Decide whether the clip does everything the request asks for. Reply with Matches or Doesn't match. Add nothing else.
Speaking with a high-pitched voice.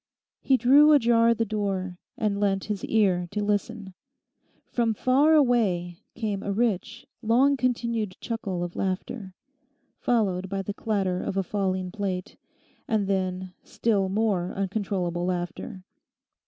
Matches